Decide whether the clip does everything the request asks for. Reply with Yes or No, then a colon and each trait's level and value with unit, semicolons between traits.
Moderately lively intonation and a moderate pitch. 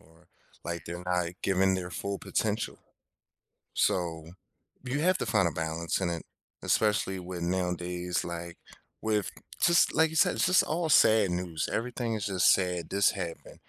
No: average, 3.8 semitones; very low, 90 Hz